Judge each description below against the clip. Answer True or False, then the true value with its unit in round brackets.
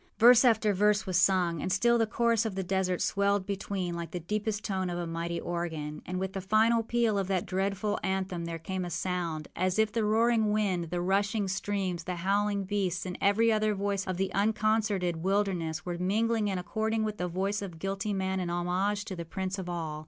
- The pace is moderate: False (210 wpm)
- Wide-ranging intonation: False (2.8 semitones)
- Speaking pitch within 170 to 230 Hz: True (190 Hz)